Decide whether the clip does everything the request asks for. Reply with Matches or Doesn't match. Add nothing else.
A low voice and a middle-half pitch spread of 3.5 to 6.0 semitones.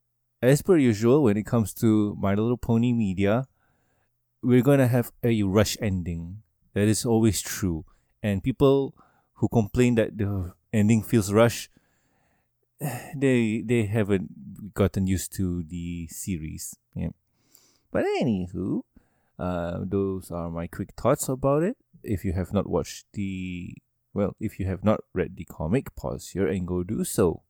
Matches